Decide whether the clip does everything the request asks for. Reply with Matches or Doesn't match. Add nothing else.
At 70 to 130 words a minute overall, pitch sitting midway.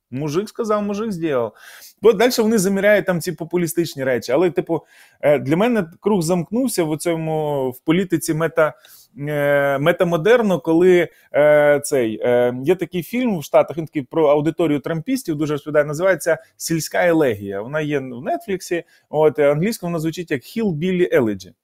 Doesn't match